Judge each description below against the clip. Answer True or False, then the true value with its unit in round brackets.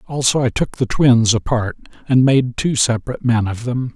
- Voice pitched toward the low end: True (120 Hz)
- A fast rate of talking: False (195 wpm)